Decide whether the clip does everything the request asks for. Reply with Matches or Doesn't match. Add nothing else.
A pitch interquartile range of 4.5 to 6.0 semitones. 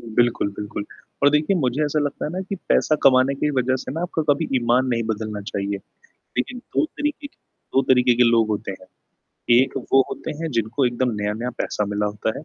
Matches